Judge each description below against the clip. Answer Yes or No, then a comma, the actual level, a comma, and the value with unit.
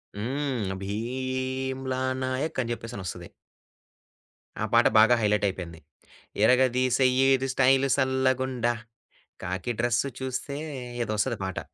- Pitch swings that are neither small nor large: Yes, average, 3.1 semitones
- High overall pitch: No, low, 130 Hz